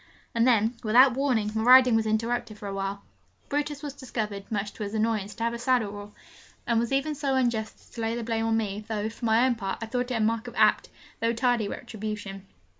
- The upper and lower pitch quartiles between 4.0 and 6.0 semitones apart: No, narrow, 2.4 semitones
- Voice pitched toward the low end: No, high, 225 Hz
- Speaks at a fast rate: Yes, fast, 235 wpm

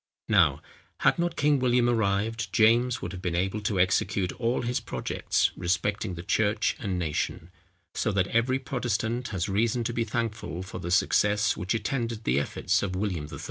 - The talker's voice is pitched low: Yes, low, 110 Hz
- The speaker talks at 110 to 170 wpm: No, average, 180 wpm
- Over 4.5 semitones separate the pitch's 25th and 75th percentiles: No, average, 4.1 semitones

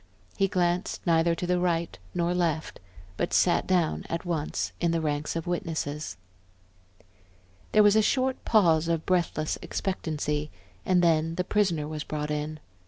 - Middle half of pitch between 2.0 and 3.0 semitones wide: Yes, narrow, 2.5 semitones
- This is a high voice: No, medium, 170 Hz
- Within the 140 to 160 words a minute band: Yes, average, 155 wpm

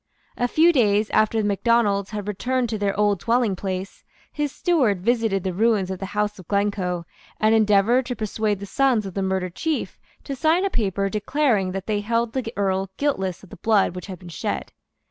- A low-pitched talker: No, high, 210 Hz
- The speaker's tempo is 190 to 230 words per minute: Yes, average, 200 wpm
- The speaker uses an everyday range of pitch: Yes, average, 3.4 semitones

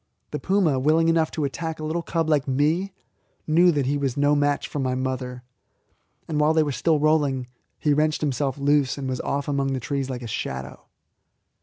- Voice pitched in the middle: Yes, medium, 145 Hz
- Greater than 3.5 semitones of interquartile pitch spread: No, average, 2.8 semitones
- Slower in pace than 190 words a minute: No, average, 200 wpm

